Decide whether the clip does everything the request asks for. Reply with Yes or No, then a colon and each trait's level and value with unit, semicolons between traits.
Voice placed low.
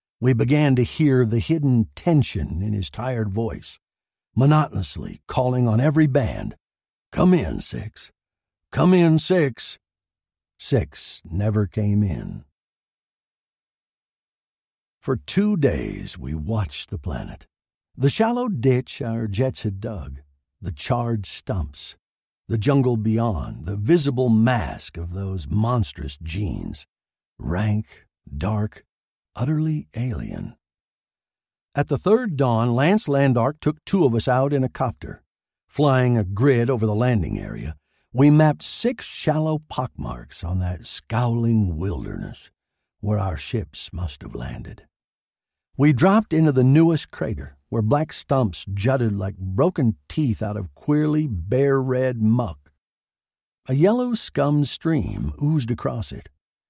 Yes: low, 115 Hz